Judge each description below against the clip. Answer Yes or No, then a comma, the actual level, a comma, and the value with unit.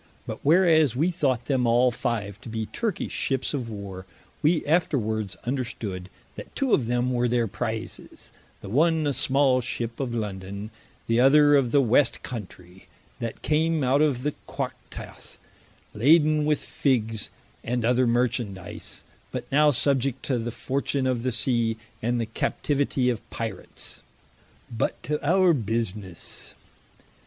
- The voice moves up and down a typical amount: Yes, average, 4.2 semitones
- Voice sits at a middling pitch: No, low, 125 Hz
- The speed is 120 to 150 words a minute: Yes, average, 145 wpm